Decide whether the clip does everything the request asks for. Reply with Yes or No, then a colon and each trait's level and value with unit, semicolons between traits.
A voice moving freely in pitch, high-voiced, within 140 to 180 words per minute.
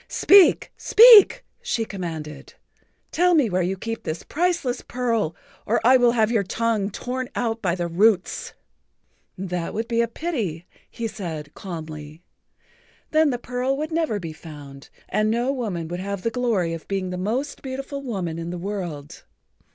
Yes: wide, 6.2 semitones; high, 215 Hz; average, 165 wpm